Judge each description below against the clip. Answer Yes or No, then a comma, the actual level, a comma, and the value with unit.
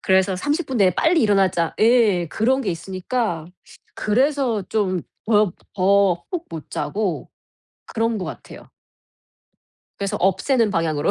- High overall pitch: Yes, high, 200 Hz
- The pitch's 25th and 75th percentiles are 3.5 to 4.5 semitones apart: Yes, average, 4.2 semitones